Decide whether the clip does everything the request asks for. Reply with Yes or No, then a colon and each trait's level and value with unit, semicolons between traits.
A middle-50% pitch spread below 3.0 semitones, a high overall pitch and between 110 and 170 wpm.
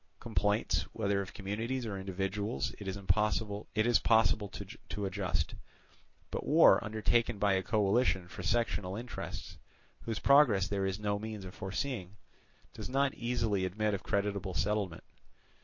No: narrow, 2.5 semitones; low, 105 Hz; slow, 135 wpm